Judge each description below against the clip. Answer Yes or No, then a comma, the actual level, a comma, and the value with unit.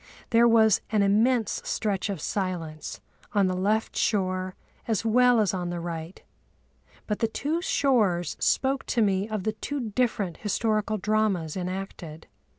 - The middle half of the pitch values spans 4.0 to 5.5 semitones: No, average, 3.4 semitones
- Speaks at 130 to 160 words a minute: Yes, average, 150 wpm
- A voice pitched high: Yes, high, 210 Hz